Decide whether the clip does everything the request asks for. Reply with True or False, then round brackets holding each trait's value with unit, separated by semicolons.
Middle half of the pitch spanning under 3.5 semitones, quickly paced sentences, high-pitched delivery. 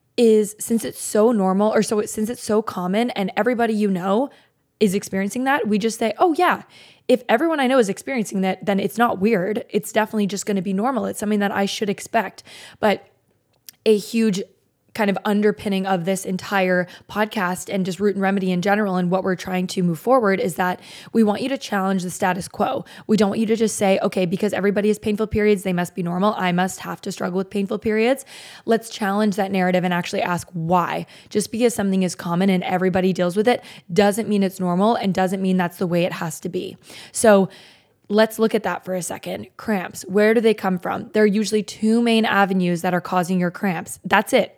True (2.6 semitones; 225 wpm; 200 Hz)